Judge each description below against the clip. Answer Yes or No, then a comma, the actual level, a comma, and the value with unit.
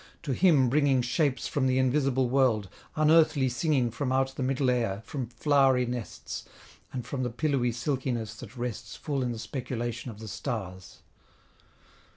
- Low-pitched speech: Yes, low, 130 Hz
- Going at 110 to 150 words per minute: No, average, 160 wpm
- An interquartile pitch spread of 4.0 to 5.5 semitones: No, narrow, 2.5 semitones